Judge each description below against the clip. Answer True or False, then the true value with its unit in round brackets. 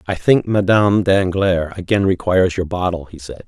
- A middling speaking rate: True (175 wpm)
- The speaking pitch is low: True (95 Hz)